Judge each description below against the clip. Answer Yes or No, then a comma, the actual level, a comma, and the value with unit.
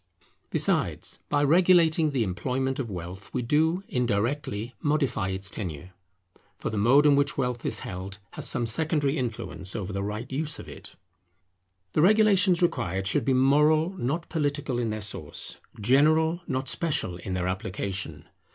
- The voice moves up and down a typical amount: No, wide, 7.0 semitones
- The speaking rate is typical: Yes, average, 155 wpm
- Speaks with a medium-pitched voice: No, low, 130 Hz